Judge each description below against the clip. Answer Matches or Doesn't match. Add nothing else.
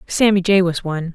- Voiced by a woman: Matches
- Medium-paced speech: Doesn't match